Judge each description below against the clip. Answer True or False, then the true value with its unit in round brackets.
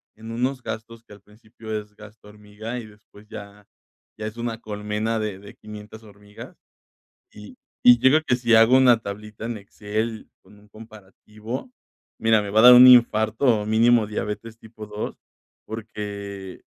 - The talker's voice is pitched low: True (110 Hz)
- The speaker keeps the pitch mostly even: True (1.7 semitones)